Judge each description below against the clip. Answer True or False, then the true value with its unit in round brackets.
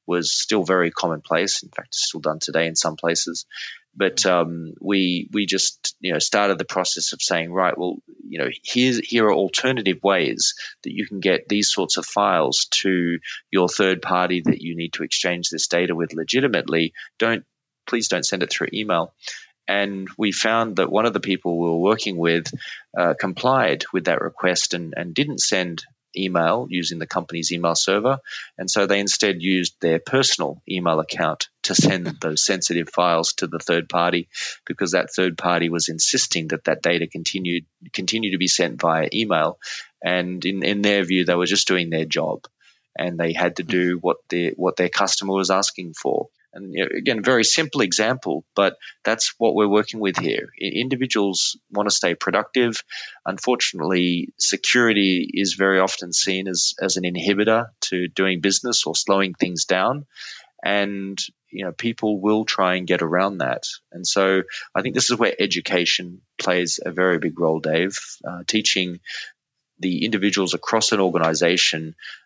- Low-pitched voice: True (90 Hz)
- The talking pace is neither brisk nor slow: True (175 wpm)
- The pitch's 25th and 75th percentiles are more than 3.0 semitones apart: False (2.6 semitones)